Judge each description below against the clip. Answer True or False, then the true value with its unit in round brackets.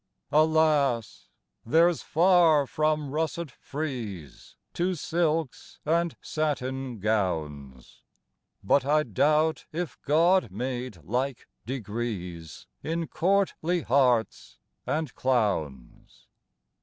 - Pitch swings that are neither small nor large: False (6.1 semitones)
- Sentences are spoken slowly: True (85 wpm)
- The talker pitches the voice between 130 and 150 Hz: True (140 Hz)